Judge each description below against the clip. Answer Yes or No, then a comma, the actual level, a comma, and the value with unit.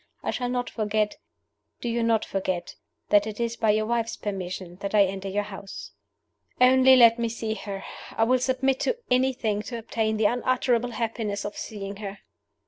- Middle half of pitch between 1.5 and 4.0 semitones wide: Yes, average, 2.9 semitones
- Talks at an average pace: Yes, average, 180 wpm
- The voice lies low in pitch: No, high, 220 Hz